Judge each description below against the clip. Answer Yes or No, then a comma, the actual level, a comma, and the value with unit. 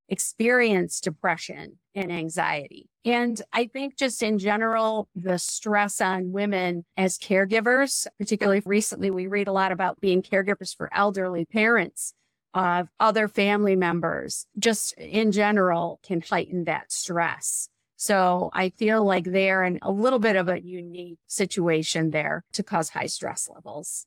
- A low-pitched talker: No, high, 195 Hz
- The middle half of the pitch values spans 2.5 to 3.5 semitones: Yes, average, 3.2 semitones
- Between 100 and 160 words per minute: Yes, average, 145 wpm